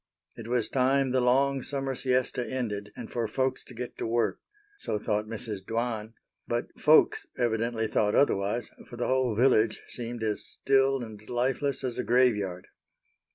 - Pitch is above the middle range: No, low, 120 Hz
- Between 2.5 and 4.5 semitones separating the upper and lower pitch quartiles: Yes, average, 2.9 semitones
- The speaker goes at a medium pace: Yes, average, 160 wpm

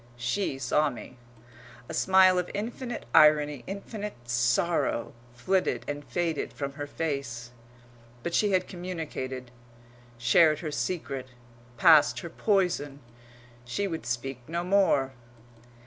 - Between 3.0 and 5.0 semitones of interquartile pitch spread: No, wide, 5.6 semitones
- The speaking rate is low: Yes, slow, 115 wpm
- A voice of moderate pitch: Yes, medium, 150 Hz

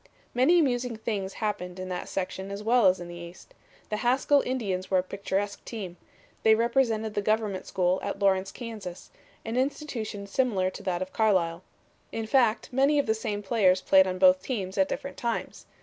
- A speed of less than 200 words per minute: Yes, average, 185 wpm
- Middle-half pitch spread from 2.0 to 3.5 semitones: No, average, 4.0 semitones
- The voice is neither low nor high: No, high, 205 Hz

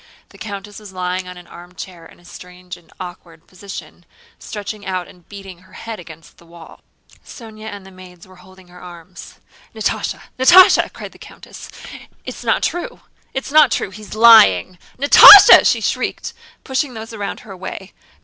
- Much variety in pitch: No, average, 3.3 semitones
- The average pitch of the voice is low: No, medium, 185 Hz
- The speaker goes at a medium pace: Yes, average, 170 wpm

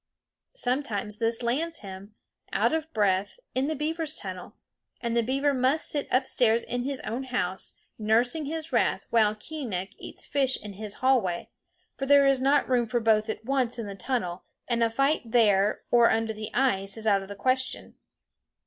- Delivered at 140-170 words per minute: No, average, 180 wpm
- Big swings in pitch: No, average, 4.3 semitones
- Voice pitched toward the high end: Yes, high, 235 Hz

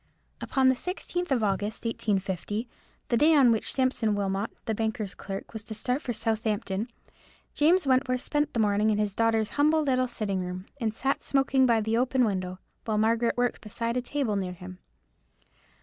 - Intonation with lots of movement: No, average, 3.8 semitones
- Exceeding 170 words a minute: Yes, average, 180 wpm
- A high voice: Yes, high, 225 Hz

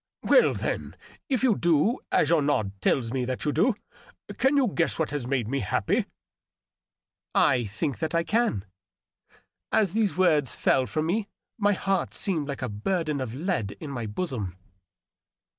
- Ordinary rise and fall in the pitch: No, wide, 7.2 semitones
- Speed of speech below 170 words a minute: No, average, 175 wpm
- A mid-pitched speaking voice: Yes, medium, 150 Hz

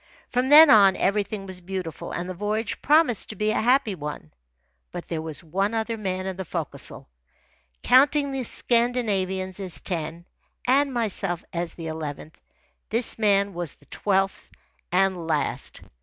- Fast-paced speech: No, average, 155 wpm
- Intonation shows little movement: No, average, 4.5 semitones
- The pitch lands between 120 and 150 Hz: No, high, 195 Hz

